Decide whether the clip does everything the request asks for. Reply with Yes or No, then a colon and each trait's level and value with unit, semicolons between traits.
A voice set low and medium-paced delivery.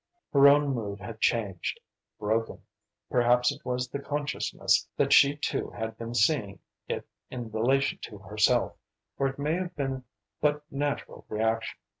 Yes: low, 125 Hz; average, 150 wpm